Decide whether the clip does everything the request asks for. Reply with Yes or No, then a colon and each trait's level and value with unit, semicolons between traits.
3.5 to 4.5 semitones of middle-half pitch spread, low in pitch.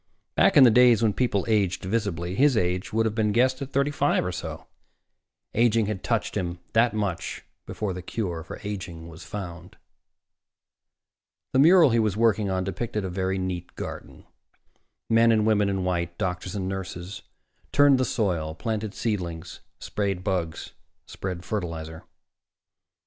Yes: average, 4.0 semitones; low, 100 Hz